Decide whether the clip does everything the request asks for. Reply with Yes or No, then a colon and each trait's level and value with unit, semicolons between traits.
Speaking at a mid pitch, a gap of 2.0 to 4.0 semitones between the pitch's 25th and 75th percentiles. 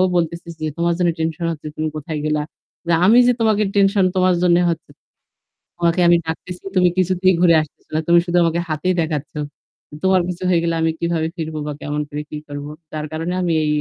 Yes: medium, 170 Hz; narrow, 2.5 semitones